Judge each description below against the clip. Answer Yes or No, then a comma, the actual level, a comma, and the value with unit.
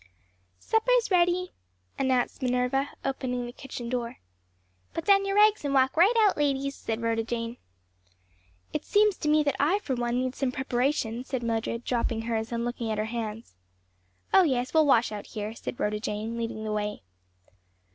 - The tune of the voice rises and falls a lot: No, average, 4.4 semitones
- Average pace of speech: Yes, average, 175 wpm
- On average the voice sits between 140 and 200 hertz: No, very high, 250 Hz